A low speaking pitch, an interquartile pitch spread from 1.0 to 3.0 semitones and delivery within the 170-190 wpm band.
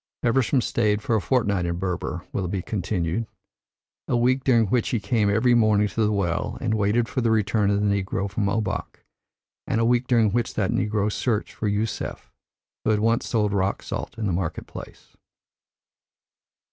Yes: low, 105 Hz; narrow, 2.5 semitones; average, 180 wpm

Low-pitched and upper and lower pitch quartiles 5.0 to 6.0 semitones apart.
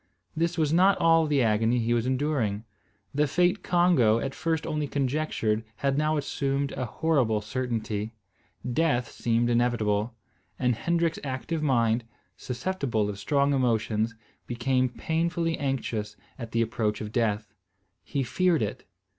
Yes: low, 130 Hz; average, 5.3 semitones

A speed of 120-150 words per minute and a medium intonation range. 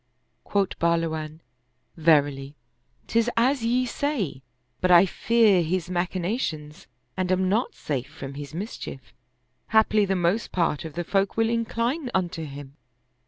No: average, 145 wpm; wide, 6.0 semitones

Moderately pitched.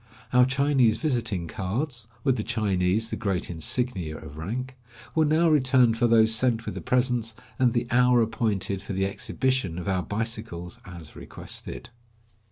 No: low, 115 Hz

